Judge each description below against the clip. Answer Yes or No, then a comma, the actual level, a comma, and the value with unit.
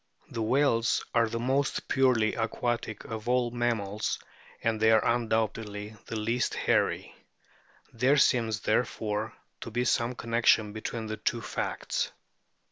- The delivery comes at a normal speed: No, slow, 130 wpm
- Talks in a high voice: No, low, 115 Hz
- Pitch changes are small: Yes, narrow, 1.8 semitones